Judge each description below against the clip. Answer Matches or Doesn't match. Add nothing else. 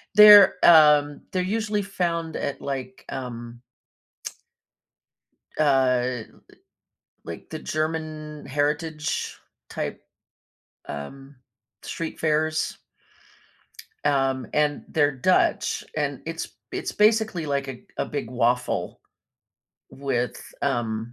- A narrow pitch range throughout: Doesn't match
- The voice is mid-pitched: Matches